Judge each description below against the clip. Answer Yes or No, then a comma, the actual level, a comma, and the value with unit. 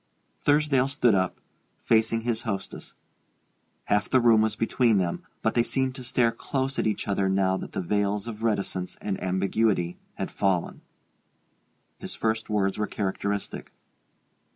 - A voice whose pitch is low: Yes, low, 110 Hz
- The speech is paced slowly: No, average, 150 wpm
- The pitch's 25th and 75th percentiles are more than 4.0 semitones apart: No, average, 3.2 semitones